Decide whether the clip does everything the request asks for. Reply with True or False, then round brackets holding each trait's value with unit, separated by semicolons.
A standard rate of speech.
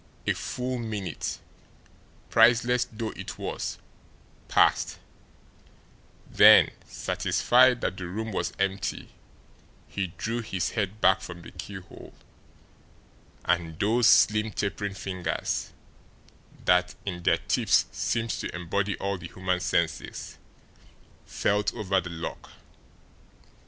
False (110 wpm)